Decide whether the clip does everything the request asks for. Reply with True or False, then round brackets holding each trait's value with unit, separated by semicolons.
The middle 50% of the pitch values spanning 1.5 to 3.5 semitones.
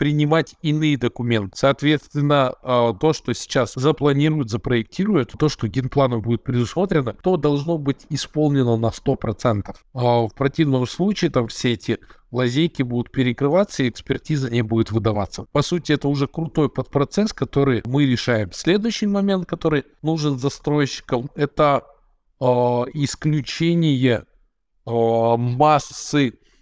False (3.9 semitones)